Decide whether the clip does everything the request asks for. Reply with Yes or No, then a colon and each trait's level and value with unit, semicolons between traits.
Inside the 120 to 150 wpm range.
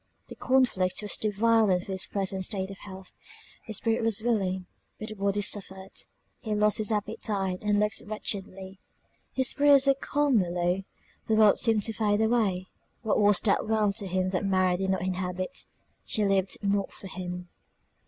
No: average, 175 wpm